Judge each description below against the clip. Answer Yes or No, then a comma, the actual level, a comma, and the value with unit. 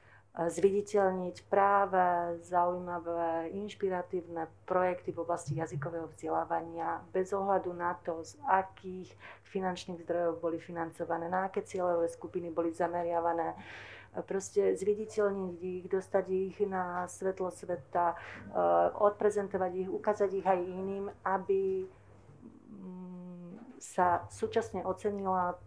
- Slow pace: Yes, slow, 100 wpm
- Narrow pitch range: Yes, narrow, 2.2 semitones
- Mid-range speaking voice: Yes, medium, 180 Hz